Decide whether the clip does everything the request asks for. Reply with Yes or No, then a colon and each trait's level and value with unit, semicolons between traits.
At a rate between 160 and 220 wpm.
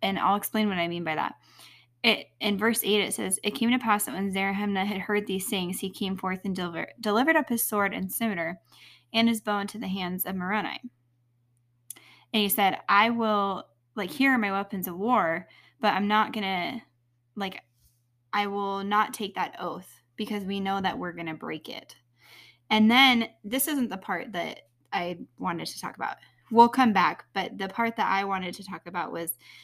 Yes: average, 200 wpm